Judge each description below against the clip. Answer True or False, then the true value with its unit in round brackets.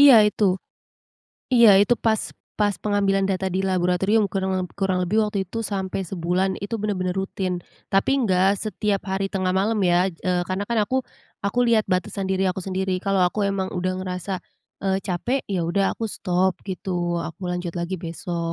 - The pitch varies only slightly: True (1.8 semitones)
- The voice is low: False (190 Hz)